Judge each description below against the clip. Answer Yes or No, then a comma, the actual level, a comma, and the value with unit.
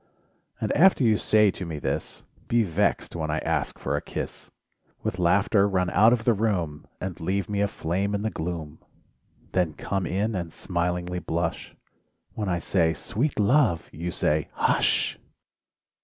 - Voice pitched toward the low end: Yes, very low, 90 Hz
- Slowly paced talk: No, average, 165 wpm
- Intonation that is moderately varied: Yes, average, 3.7 semitones